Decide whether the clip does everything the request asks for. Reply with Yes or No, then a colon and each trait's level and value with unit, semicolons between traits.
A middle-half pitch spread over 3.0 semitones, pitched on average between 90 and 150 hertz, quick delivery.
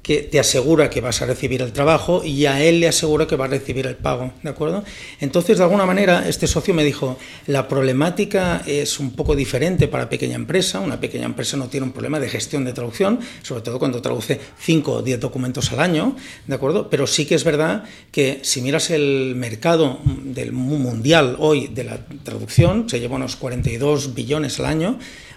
Yes: average, 3.6 semitones; medium, 140 Hz; fast, 200 wpm